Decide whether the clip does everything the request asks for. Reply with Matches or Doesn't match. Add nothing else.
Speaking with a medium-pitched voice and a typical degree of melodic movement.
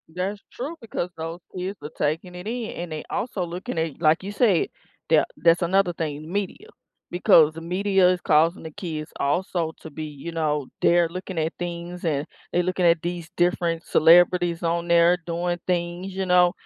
Doesn't match